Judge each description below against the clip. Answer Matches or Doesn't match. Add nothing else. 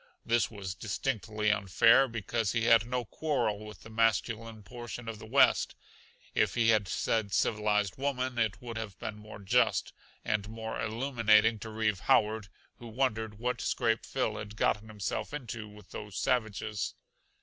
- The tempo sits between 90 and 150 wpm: Doesn't match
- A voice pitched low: Matches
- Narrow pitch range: Matches